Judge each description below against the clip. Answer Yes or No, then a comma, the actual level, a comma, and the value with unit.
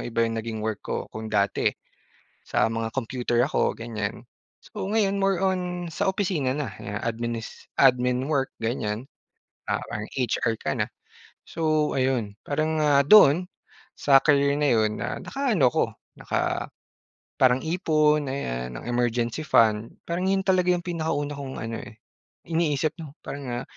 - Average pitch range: No, wide, 5.7 semitones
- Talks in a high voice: No, low, 135 Hz